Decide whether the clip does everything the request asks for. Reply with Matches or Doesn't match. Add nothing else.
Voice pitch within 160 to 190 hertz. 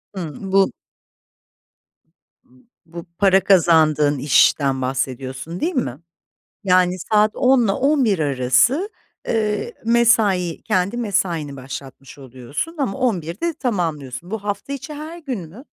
Matches